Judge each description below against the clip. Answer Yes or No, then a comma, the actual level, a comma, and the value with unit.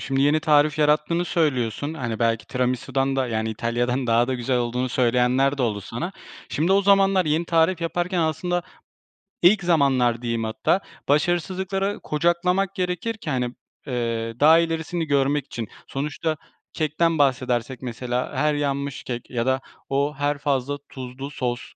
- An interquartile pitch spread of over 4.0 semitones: Yes, average, 5.0 semitones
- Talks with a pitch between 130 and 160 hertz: Yes, medium, 140 Hz